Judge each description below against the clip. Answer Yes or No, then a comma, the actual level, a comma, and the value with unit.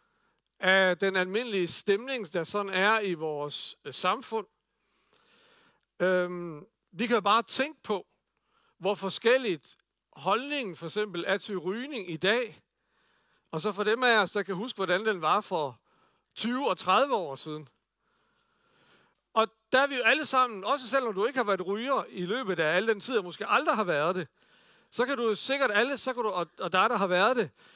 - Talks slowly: No, average, 185 wpm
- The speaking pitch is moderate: No, high, 215 Hz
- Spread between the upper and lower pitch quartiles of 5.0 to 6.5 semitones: Yes, average, 5.3 semitones